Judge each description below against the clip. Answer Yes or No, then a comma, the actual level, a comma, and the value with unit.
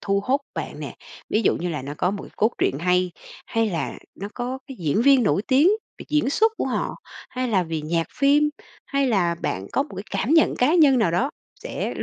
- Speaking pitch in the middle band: No, high, 220 Hz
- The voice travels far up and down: Yes, wide, 7.5 semitones